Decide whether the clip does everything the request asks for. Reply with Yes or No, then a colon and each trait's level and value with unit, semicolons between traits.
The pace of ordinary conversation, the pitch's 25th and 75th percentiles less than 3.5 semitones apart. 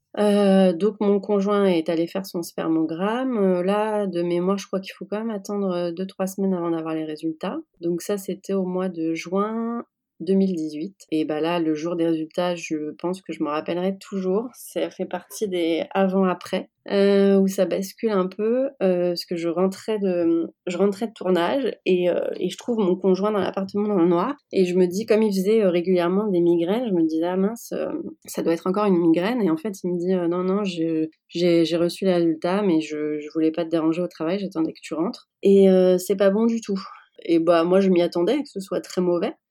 No: fast, 225 wpm; narrow, 2.6 semitones